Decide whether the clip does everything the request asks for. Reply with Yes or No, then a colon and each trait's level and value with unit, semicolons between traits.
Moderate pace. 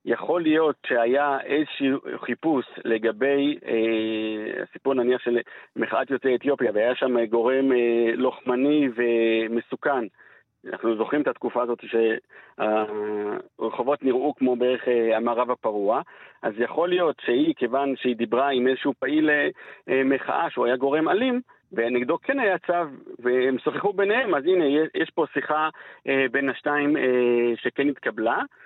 Yes: average, 140 wpm